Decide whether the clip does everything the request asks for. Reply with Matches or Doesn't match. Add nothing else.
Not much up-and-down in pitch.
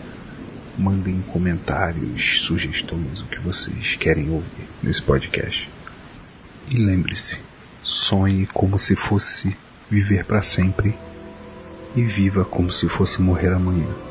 Matches